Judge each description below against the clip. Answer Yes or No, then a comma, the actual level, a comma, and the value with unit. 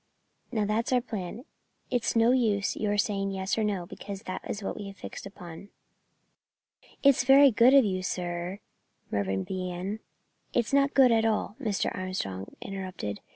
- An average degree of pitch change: Yes, average, 3.8 semitones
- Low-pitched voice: No, high, 205 Hz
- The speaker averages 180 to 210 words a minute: No, average, 160 wpm